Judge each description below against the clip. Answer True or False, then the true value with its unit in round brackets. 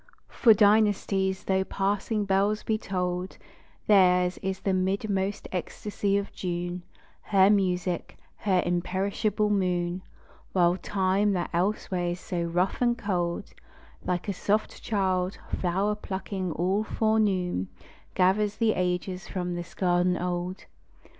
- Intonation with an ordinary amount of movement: False (2.2 semitones)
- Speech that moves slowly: True (120 wpm)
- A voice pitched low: False (190 Hz)